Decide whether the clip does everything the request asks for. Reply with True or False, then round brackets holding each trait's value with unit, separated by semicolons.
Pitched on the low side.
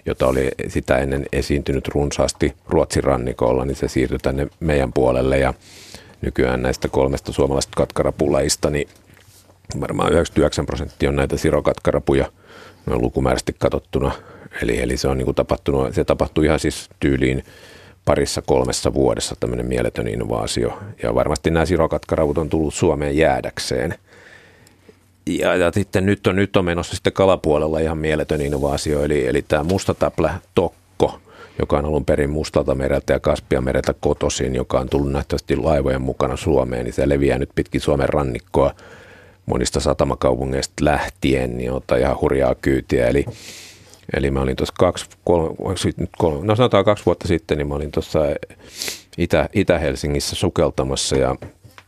True (70 Hz)